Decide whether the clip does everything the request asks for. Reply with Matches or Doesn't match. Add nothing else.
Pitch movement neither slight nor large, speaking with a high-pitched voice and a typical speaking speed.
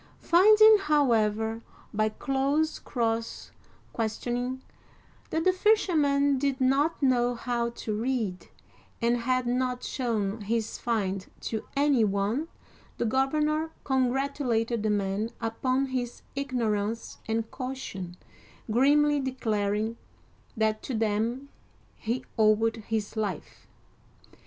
Doesn't match